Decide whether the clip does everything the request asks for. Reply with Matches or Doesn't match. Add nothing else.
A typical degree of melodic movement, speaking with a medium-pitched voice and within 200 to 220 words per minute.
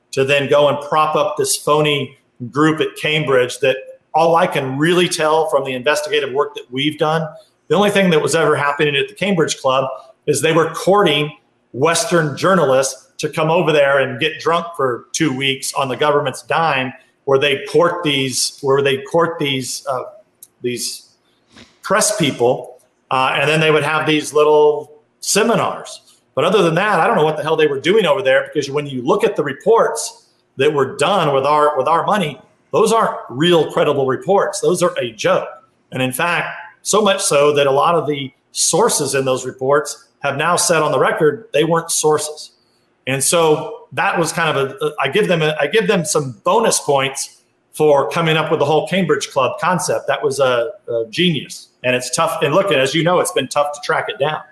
Matches